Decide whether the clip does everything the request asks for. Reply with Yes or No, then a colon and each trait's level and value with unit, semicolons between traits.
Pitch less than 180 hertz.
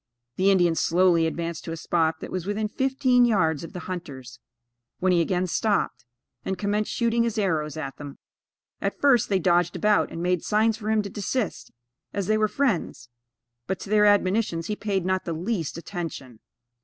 No: medium, 185 Hz